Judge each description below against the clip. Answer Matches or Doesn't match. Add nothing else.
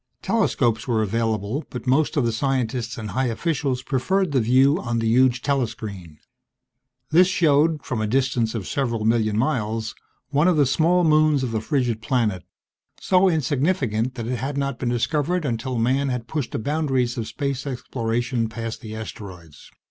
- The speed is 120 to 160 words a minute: Doesn't match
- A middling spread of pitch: Matches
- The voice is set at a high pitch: Doesn't match